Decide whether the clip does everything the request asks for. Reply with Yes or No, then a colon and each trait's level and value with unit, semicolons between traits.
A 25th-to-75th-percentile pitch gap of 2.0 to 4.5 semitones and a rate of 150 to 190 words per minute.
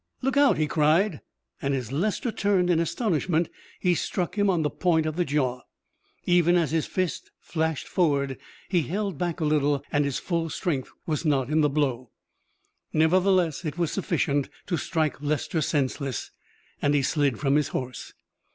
Yes: average, 3.7 semitones; average, 170 wpm